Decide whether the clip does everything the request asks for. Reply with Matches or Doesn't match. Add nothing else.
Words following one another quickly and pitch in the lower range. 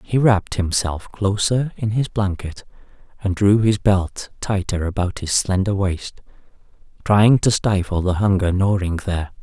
Doesn't match